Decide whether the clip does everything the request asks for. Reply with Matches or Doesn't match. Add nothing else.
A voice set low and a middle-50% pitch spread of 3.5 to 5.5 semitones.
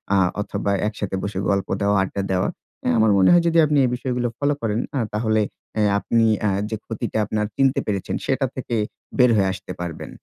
Matches